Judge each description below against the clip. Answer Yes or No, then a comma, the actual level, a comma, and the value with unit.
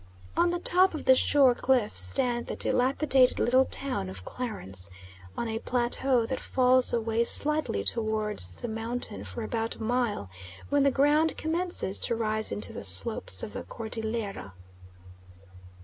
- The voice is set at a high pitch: Yes, high, 235 Hz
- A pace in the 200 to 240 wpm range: No, average, 150 wpm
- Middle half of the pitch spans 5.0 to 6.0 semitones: No, average, 3.8 semitones